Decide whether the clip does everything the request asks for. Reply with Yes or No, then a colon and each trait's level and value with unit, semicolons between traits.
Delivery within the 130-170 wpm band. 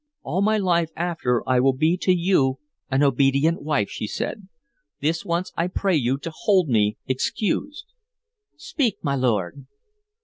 Yes: average, 150 wpm